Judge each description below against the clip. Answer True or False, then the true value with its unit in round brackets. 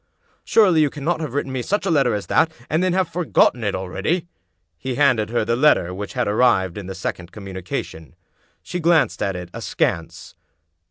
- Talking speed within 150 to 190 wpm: False (200 wpm)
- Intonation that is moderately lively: False (8.6 semitones)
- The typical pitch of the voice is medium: False (125 Hz)